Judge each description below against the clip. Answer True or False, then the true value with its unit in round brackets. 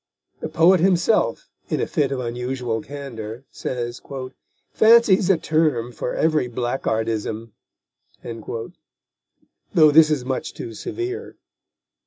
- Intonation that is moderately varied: False (5.7 semitones)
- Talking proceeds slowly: True (110 wpm)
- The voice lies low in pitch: True (130 Hz)